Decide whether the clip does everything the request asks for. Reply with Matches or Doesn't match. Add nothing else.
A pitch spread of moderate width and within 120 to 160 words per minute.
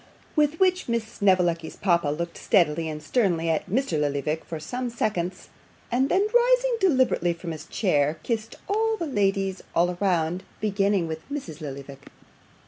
Doesn't match